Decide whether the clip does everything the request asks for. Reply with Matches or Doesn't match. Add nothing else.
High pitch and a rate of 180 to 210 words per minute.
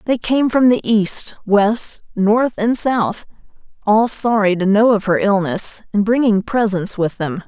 Doesn't match